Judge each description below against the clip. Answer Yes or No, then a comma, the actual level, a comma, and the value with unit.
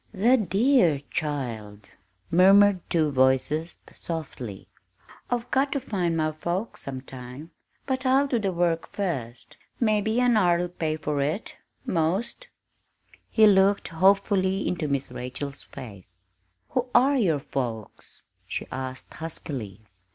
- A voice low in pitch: No, medium, 170 Hz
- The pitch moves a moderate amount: No, wide, 7.0 semitones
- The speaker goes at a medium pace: No, slow, 120 wpm